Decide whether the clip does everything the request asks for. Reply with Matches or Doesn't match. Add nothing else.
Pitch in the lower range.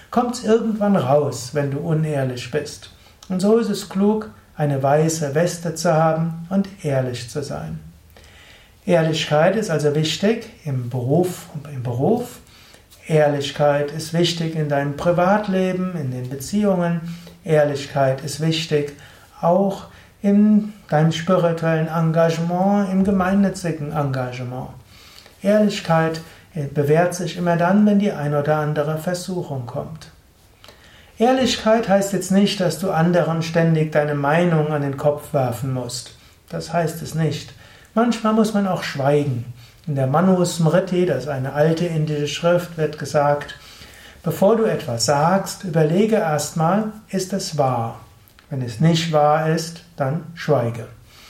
Doesn't match